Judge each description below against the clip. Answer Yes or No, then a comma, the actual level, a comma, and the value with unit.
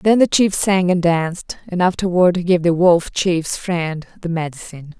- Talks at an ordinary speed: Yes, average, 190 wpm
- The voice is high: No, medium, 175 Hz